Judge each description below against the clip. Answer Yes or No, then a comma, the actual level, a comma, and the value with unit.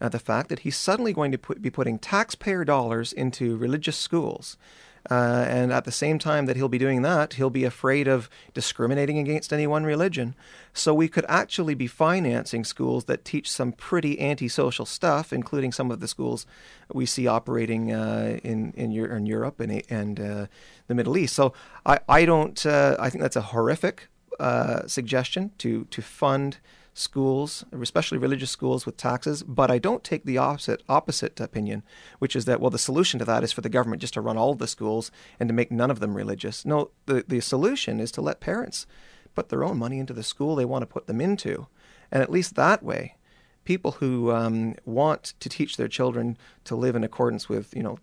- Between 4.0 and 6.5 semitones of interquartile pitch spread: Yes, average, 4.3 semitones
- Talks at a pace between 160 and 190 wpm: No, fast, 205 wpm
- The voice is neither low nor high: No, low, 130 Hz